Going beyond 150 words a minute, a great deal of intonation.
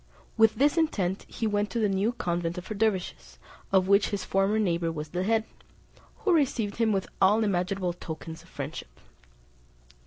No: average, 165 wpm; average, 3.8 semitones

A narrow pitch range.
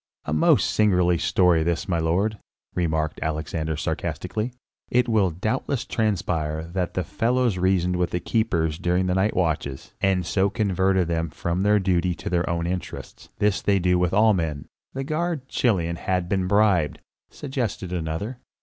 No: average, 3.7 semitones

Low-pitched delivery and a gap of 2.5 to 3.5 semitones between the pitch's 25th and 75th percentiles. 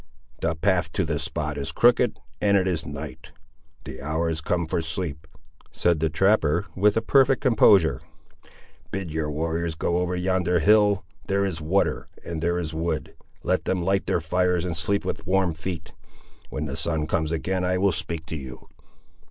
Yes: very low, 85 Hz; average, 3.0 semitones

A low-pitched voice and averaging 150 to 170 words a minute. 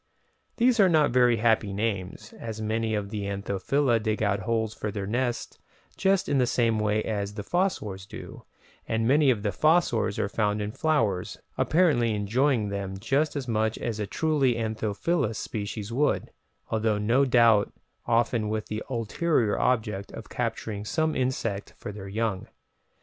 Yes: low, 110 Hz; average, 160 wpm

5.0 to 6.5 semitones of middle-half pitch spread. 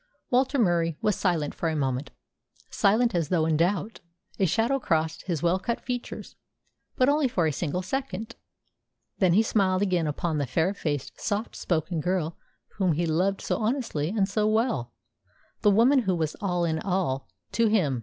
Yes: average, 5.3 semitones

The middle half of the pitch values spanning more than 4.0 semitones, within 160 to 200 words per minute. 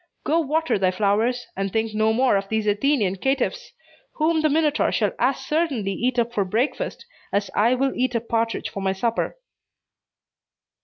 Yes: average, 5.0 semitones; average, 170 wpm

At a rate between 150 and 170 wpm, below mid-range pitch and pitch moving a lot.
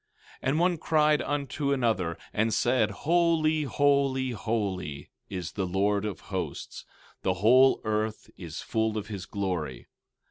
No: average, 140 wpm; low, 110 Hz; wide, 6.5 semitones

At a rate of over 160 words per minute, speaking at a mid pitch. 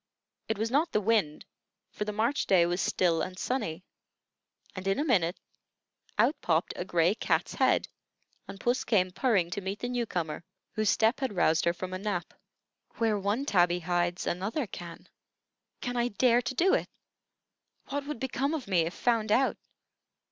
No: average, 175 wpm; high, 205 Hz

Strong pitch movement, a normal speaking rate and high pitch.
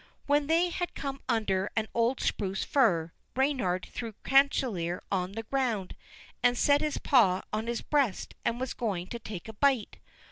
Yes: wide, 5.9 semitones; average, 170 wpm; high, 235 Hz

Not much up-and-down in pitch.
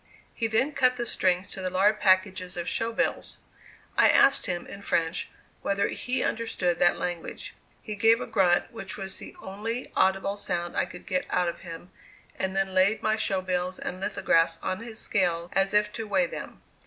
No: average, 3.1 semitones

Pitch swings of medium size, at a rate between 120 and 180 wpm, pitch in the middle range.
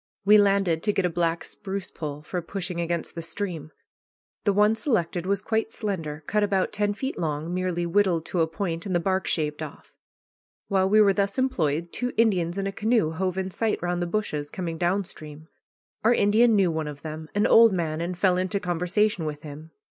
No: average, 3.7 semitones; fast, 205 wpm; medium, 180 Hz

